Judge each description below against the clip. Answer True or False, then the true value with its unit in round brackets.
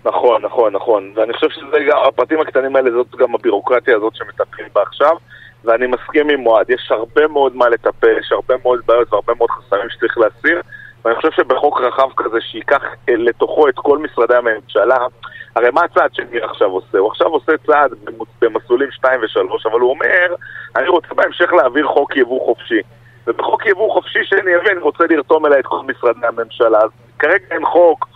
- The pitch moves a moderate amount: False (8.2 semitones)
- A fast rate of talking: True (180 wpm)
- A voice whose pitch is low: False (150 Hz)